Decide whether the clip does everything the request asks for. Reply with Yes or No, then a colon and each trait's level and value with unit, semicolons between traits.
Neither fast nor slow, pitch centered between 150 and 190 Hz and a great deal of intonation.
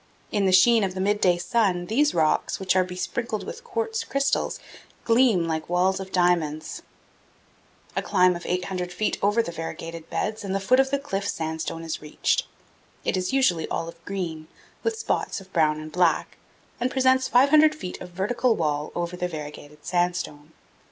Yes: average, 175 wpm; medium, 185 Hz; wide, 5.7 semitones